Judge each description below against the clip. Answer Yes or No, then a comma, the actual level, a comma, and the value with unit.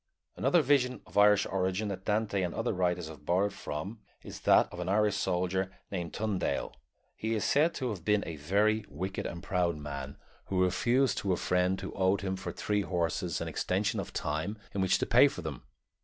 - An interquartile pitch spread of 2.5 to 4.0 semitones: Yes, average, 2.9 semitones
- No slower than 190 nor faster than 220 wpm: Yes, average, 200 wpm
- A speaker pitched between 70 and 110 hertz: Yes, very low, 95 Hz